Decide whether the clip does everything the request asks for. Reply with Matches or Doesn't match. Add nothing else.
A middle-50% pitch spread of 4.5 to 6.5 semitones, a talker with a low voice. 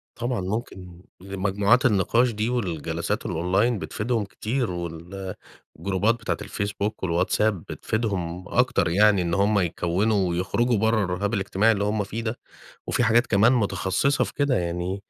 Doesn't match